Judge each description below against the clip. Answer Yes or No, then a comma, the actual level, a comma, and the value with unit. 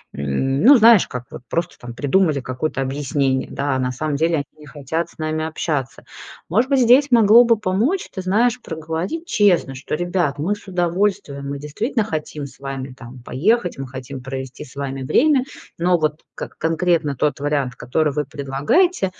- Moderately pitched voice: Yes, medium, 155 Hz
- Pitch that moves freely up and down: Yes, wide, 5.9 semitones